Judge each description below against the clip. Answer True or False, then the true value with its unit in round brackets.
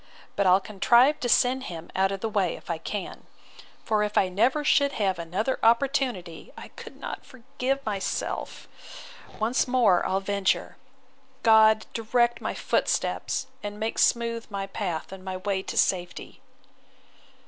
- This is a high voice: True (210 Hz)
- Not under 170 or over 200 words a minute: False (150 wpm)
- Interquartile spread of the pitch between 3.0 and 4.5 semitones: True (4.0 semitones)